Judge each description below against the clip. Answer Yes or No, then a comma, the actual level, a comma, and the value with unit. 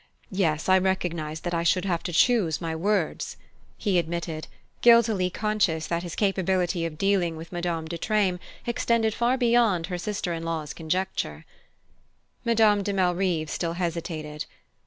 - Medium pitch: Yes, medium, 180 Hz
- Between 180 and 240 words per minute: No, average, 150 wpm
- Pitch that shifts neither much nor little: Yes, average, 3.4 semitones